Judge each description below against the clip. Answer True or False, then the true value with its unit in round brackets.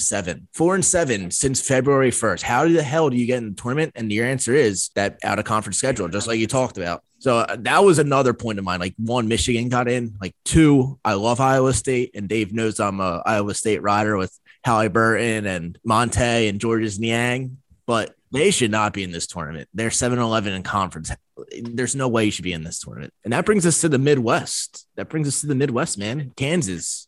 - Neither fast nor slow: False (225 wpm)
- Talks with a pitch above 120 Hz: False (115 Hz)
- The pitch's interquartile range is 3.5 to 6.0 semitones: True (4.1 semitones)